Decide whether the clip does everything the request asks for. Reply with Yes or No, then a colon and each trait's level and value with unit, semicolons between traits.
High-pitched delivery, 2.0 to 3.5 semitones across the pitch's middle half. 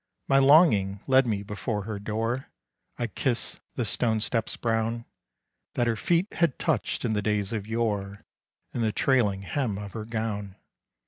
No: low, 110 Hz; average, 2.8 semitones